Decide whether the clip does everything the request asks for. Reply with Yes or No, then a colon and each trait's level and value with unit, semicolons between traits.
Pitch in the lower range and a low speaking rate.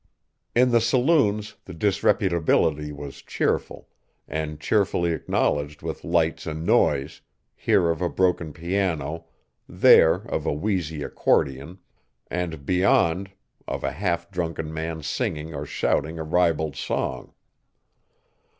Yes: very low, 85 Hz; slow, 120 wpm